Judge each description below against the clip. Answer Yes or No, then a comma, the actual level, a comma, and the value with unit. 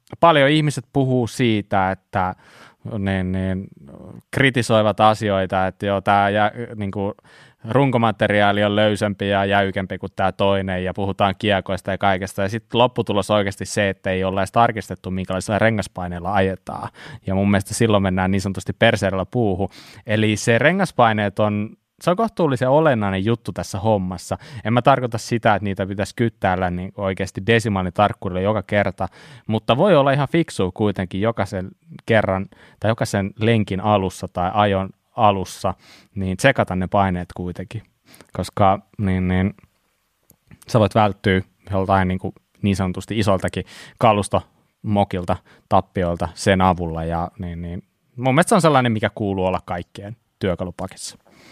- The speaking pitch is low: Yes, low, 100 Hz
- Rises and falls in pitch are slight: No, average, 3.1 semitones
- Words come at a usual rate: Yes, average, 145 wpm